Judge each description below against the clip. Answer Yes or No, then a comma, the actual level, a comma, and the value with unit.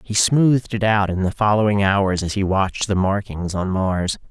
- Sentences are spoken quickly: Yes, fast, 210 wpm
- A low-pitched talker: Yes, low, 100 Hz